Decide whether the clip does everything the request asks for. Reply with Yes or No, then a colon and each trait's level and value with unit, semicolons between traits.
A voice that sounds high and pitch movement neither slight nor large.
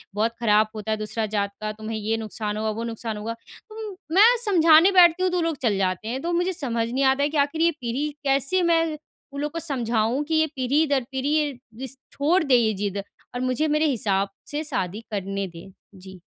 No: very high, 255 Hz; wide, 6.4 semitones